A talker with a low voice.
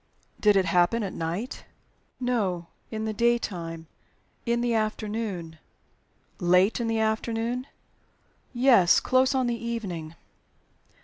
No: high, 220 Hz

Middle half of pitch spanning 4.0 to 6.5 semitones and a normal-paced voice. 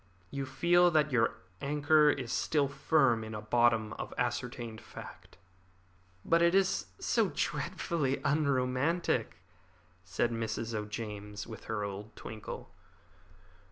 No: average, 5.1 semitones; slow, 120 wpm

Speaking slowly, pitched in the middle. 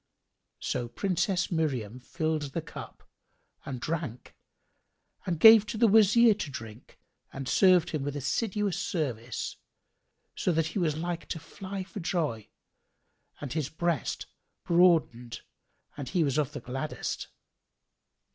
Yes: slow, 130 wpm; medium, 160 Hz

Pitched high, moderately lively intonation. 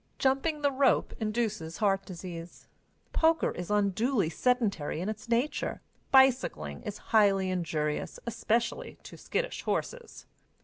No: high, 215 Hz; wide, 6.2 semitones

